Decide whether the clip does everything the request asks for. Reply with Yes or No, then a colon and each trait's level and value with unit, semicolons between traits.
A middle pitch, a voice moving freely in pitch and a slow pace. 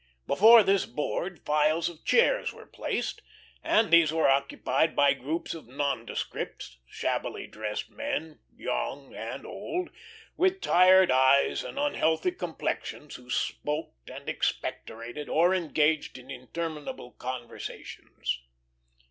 Yes: medium, 155 Hz; wide, 5.7 semitones; slow, 115 wpm